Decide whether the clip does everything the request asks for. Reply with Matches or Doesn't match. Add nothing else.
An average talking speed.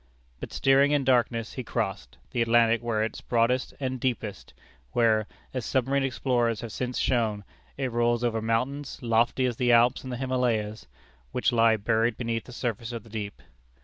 Matches